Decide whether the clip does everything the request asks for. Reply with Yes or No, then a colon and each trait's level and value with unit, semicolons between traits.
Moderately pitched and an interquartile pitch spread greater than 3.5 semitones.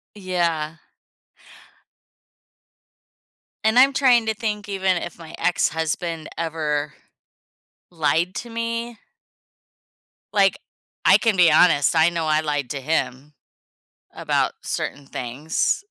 Yes: medium, 170 Hz; average, 5.3 semitones